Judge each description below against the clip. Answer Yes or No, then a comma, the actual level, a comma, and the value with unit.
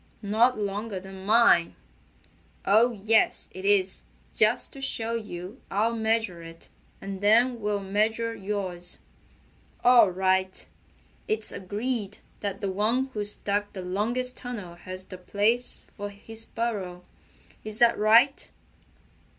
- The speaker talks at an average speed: No, slow, 125 wpm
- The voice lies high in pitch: Yes, high, 210 Hz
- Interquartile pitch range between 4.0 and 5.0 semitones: No, average, 3.2 semitones